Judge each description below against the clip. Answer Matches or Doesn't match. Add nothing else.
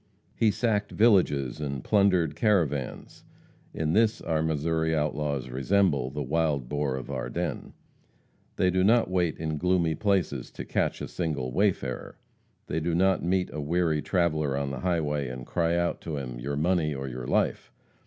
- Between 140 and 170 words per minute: Matches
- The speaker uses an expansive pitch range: Doesn't match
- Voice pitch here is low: Matches